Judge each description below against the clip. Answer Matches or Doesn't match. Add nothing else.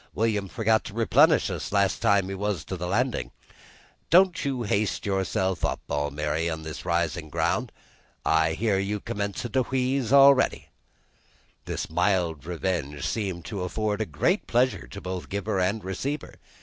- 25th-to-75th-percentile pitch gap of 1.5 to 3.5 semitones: Doesn't match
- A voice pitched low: Matches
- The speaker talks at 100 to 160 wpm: Matches